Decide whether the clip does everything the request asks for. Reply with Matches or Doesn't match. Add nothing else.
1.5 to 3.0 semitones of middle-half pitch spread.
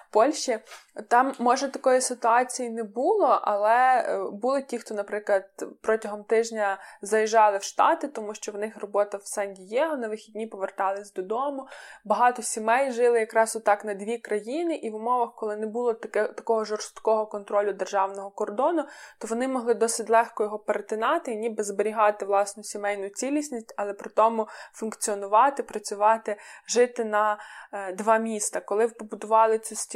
Matches